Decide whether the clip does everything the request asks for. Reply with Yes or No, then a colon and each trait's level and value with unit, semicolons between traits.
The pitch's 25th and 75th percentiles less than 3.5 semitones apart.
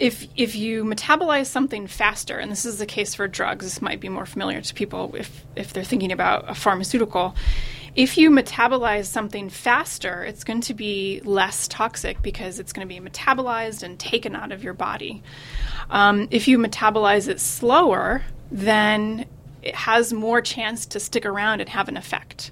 Yes: average, 2.8 semitones